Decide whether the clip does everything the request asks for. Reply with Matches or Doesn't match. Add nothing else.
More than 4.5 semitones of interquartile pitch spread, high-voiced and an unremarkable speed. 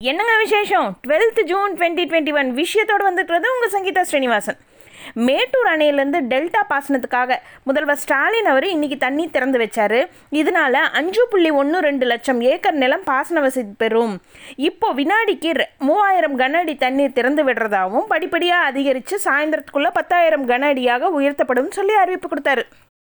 Doesn't match